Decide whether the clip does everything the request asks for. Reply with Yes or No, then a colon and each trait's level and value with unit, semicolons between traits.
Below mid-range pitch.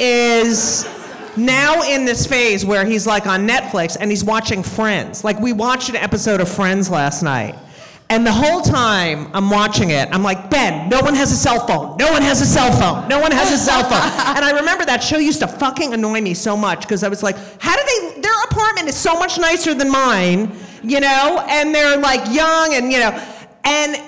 No: high, 235 Hz